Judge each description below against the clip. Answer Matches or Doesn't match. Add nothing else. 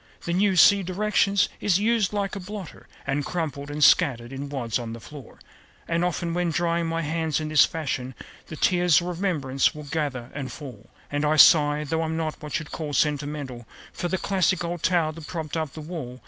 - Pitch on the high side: Doesn't match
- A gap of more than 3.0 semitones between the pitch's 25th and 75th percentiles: Matches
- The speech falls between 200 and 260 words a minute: Matches